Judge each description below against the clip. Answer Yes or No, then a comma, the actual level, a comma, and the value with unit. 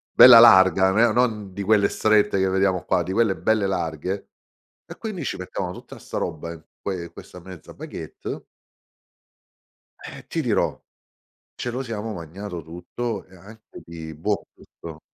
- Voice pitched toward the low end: Yes, very low, 95 Hz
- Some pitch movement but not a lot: Yes, average, 3.6 semitones